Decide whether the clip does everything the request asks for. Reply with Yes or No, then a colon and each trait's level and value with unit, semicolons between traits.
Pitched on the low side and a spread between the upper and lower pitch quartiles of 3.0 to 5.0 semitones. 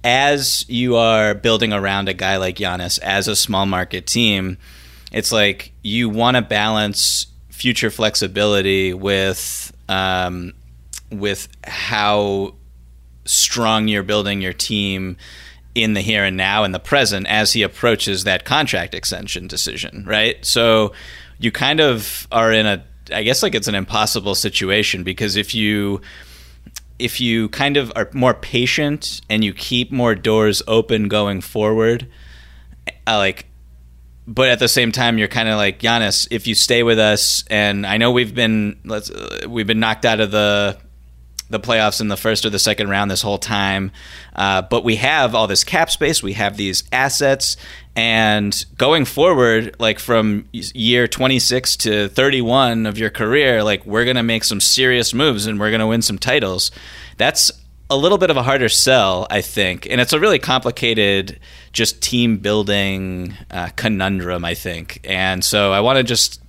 Yes: low, 105 Hz; average, 3.3 semitones